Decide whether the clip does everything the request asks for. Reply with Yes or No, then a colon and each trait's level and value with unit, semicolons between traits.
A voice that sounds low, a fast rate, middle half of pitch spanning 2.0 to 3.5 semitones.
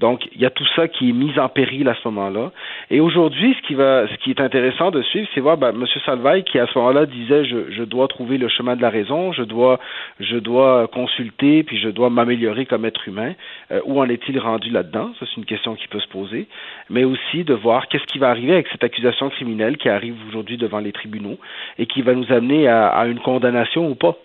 Yes: low, 125 Hz; fast, 245 wpm; average, 2.7 semitones